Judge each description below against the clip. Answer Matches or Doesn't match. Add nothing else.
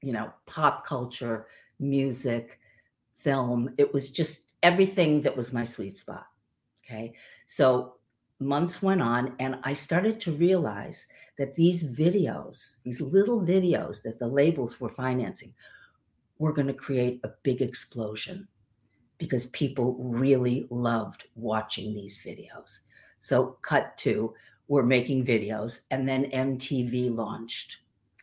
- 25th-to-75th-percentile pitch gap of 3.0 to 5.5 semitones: Matches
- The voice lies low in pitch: Matches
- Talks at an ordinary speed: Doesn't match